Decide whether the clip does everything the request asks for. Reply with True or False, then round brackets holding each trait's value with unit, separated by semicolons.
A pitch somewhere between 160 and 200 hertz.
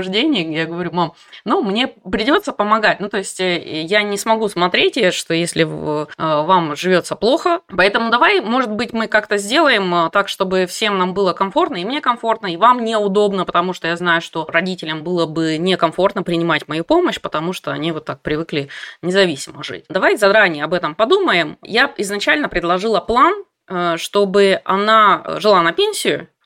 True (190 Hz)